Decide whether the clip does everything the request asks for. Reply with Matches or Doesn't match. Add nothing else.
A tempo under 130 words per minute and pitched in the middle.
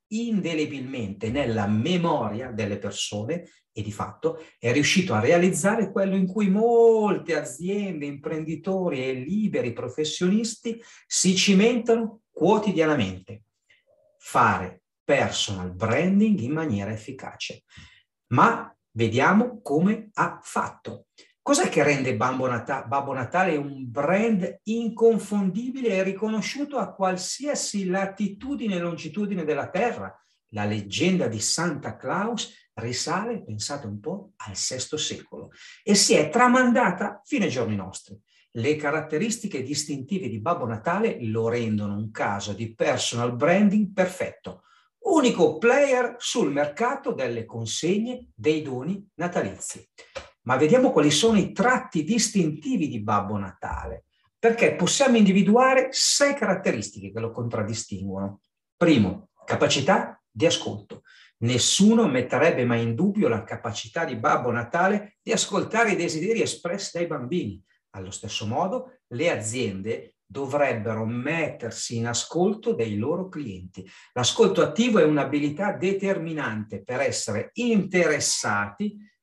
Matches